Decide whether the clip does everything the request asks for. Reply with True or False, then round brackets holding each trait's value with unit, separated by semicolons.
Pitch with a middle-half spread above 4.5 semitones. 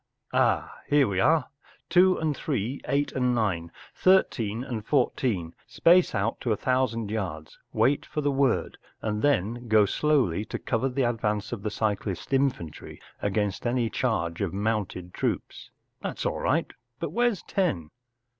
True (5.3 semitones)